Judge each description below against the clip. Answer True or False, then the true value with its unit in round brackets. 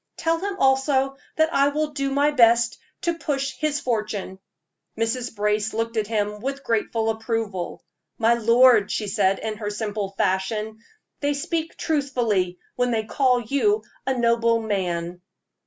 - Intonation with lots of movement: False (4.5 semitones)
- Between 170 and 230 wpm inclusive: False (150 wpm)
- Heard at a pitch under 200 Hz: False (230 Hz)